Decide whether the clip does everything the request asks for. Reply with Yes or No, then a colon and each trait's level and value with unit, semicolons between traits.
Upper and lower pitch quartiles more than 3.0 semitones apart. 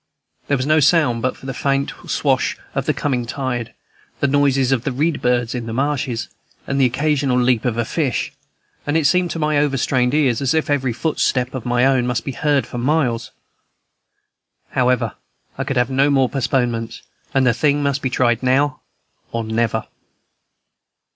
No: narrow, 2.6 semitones